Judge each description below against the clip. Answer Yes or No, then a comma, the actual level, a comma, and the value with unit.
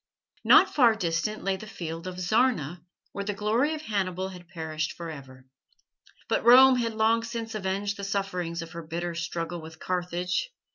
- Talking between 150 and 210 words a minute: Yes, average, 175 wpm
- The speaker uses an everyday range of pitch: Yes, average, 4.5 semitones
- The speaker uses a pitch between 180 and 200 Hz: Yes, medium, 185 Hz